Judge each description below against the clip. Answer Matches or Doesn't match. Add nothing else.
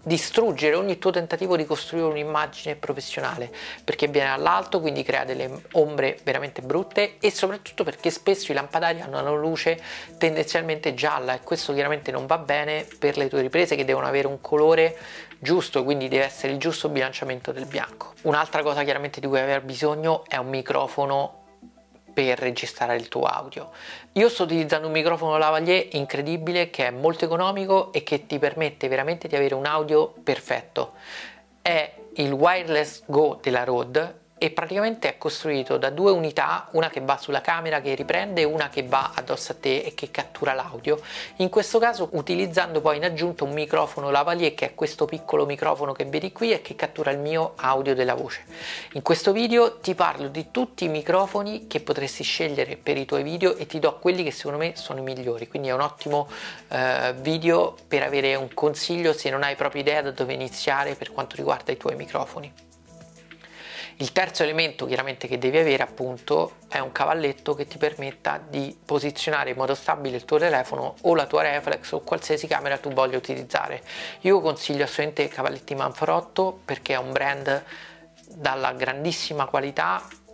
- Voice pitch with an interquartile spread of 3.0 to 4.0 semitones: Matches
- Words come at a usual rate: Doesn't match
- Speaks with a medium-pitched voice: Matches